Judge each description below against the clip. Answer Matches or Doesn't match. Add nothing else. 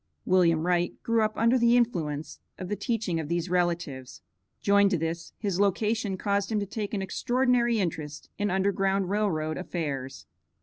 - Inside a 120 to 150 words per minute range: Doesn't match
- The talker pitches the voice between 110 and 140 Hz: Doesn't match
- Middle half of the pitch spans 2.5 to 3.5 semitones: Doesn't match